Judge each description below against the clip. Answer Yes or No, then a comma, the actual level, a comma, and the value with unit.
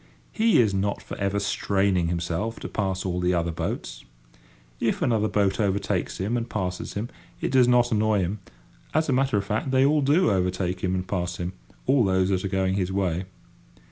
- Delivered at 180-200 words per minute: Yes, average, 195 wpm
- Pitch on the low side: Yes, low, 100 Hz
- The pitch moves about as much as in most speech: Yes, average, 3.7 semitones